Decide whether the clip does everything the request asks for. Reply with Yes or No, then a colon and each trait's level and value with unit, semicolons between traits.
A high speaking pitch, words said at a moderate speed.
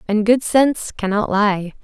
Yes: high, 215 Hz; average, 165 wpm